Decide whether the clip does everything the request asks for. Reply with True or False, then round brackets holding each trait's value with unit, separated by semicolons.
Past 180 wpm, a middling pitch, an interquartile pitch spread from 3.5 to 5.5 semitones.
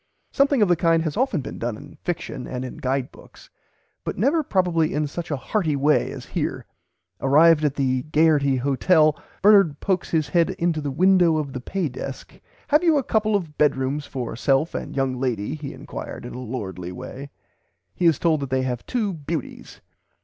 True (195 wpm; 150 Hz; 4.6 semitones)